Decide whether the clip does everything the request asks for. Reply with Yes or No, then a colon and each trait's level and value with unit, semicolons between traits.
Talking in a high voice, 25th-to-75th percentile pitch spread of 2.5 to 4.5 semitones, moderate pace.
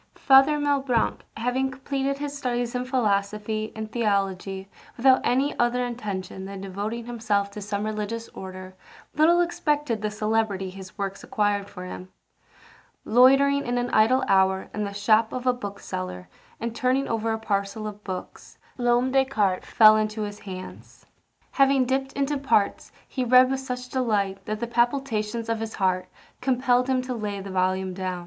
Yes: high, 225 Hz; average, 4.2 semitones; average, 165 wpm